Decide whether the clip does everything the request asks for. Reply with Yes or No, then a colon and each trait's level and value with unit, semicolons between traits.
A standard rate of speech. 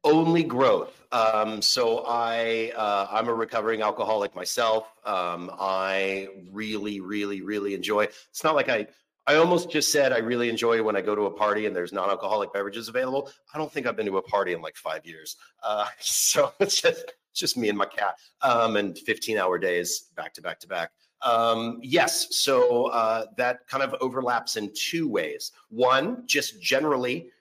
Yes: average, 180 wpm